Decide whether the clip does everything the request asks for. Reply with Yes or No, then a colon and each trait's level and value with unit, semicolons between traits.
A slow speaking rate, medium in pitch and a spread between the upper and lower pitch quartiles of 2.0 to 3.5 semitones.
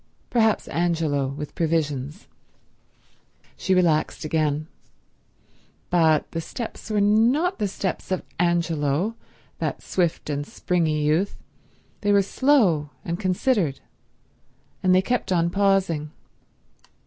No: slow, 110 wpm; medium, 175 Hz; average, 4.6 semitones